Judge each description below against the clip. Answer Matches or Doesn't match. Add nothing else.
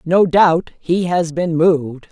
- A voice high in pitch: Doesn't match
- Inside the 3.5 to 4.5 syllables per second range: Matches